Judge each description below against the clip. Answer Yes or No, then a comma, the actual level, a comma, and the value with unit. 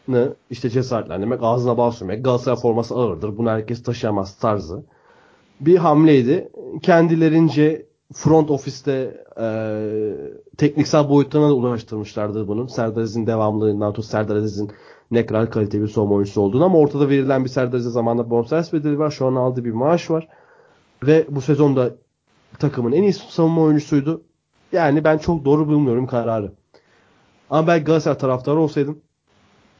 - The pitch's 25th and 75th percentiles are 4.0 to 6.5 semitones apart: Yes, average, 5.2 semitones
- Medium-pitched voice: No, low, 130 Hz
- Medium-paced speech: No, fast, 145 wpm